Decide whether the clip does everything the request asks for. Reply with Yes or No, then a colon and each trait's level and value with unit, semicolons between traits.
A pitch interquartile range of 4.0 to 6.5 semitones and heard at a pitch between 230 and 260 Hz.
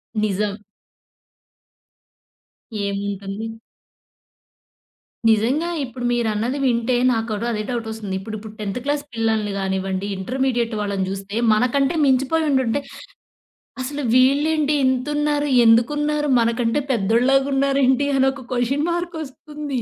Yes: average, 4.5 semitones; high, 245 Hz